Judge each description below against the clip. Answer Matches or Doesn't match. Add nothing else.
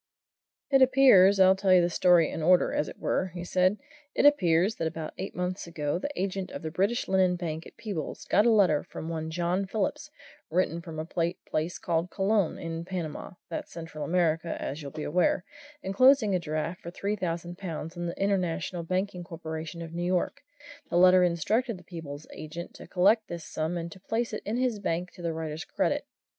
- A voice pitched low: Doesn't match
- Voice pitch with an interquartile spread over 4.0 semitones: Doesn't match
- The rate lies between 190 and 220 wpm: Matches